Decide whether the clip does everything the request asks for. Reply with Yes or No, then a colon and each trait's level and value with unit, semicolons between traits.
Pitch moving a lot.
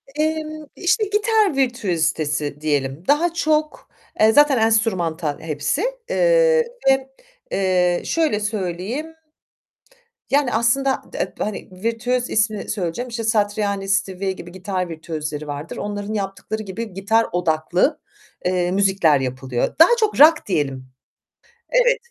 Yes: wide, 7.9 semitones